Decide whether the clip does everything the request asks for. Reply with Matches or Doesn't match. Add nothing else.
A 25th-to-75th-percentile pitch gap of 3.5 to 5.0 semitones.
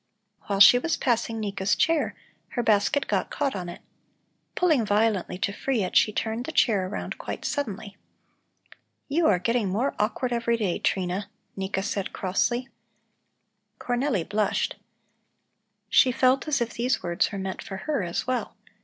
Matches